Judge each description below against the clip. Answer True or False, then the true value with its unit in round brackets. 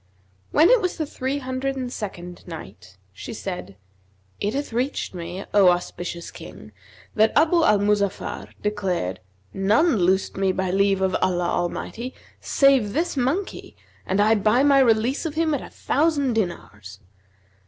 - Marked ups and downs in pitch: True (6.8 semitones)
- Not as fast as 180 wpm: True (155 wpm)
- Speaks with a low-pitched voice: False (210 Hz)